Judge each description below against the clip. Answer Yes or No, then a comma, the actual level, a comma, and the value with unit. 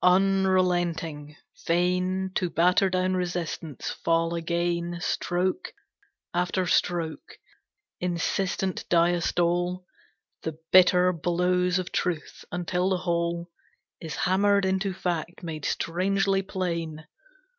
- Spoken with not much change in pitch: Yes, narrow, 1.5 semitones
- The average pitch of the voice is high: No, medium, 180 Hz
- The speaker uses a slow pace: Yes, slow, 95 wpm